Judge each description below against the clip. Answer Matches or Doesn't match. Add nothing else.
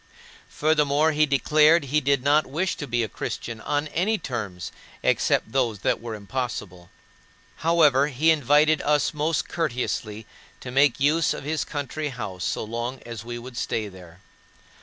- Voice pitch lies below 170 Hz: Matches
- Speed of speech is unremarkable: Matches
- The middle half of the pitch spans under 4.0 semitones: Doesn't match